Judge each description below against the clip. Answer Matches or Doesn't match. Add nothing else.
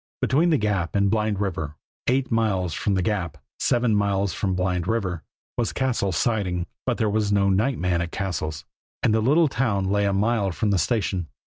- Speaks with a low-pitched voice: Matches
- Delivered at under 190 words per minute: Doesn't match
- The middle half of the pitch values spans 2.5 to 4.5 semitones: Matches